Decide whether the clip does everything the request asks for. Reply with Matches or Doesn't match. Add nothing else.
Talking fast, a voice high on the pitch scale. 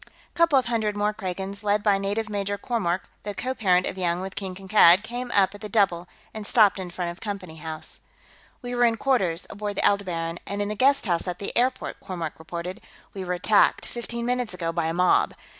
Matches